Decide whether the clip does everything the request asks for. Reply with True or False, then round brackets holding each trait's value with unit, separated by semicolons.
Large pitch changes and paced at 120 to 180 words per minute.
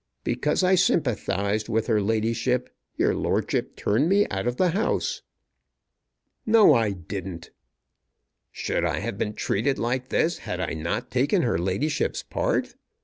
True (6.4 semitones; 145 wpm)